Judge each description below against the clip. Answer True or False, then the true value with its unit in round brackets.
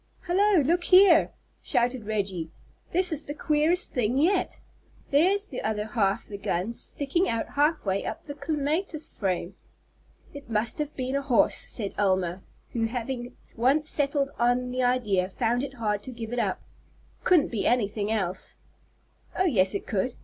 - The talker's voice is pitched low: False (250 Hz)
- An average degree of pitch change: False (6.0 semitones)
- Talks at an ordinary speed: True (165 wpm)